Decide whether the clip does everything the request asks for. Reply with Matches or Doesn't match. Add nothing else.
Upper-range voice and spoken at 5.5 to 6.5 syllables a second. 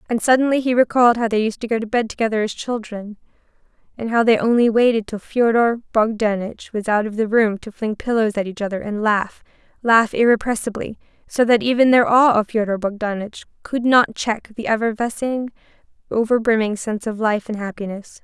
Matches